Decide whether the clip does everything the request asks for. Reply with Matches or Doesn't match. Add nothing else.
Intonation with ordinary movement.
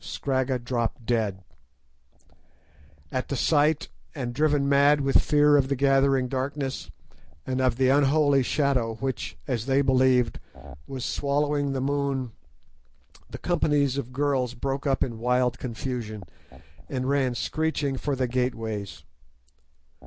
Doesn't match